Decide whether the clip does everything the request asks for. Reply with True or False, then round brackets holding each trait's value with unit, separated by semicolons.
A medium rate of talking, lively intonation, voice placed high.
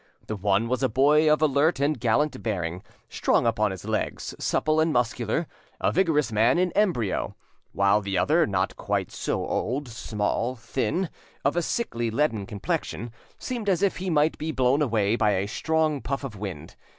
False (175 wpm; 6.5 semitones; 125 Hz)